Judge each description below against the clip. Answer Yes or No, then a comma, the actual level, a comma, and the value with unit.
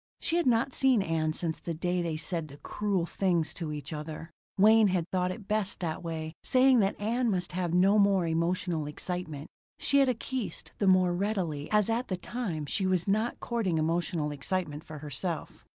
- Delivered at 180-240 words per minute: Yes, average, 190 wpm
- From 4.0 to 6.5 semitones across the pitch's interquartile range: Yes, average, 4.5 semitones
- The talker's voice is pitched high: No, medium, 180 Hz